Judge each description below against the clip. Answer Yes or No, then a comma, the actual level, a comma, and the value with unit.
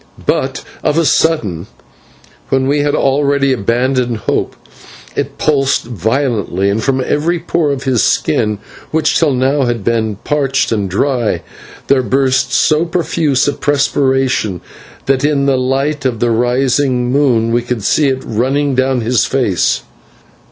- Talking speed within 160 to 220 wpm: No, average, 145 wpm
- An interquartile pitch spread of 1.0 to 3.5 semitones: Yes, average, 3.2 semitones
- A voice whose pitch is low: Yes, low, 130 Hz